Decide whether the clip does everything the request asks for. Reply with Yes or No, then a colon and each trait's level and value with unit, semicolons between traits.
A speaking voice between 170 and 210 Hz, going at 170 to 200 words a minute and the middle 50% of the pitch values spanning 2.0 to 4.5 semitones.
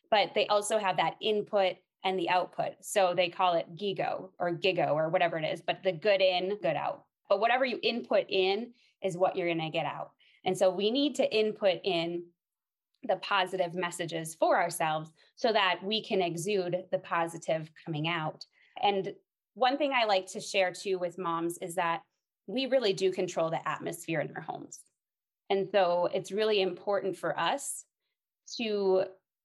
Yes: high, 190 Hz; average, 180 wpm; average, 2.9 semitones